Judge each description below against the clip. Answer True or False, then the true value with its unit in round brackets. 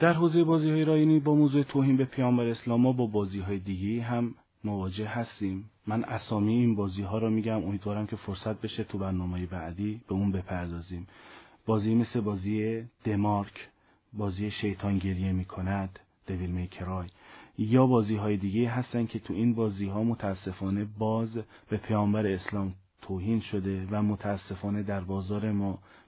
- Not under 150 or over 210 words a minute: True (155 wpm)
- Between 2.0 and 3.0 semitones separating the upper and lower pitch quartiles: True (2.7 semitones)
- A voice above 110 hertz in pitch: False (105 Hz)